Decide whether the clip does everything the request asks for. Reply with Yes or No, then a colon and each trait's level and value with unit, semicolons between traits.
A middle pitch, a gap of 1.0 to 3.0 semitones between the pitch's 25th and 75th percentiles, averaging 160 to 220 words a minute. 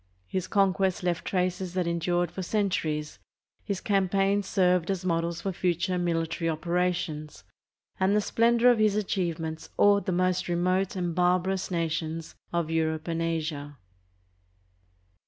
No: medium, 180 Hz; narrow, 2.4 semitones; slow, 135 wpm